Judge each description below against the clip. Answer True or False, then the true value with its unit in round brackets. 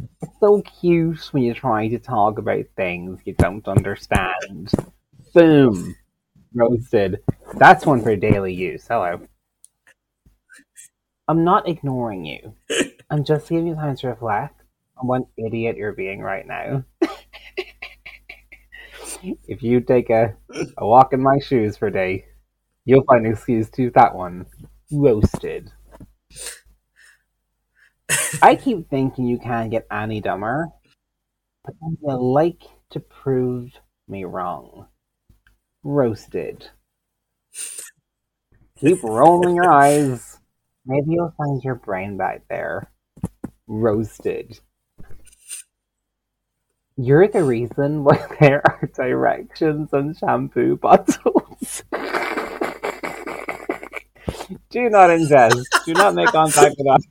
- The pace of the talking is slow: True (110 wpm)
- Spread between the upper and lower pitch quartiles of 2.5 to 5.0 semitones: False (5.4 semitones)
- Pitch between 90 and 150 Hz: True (135 Hz)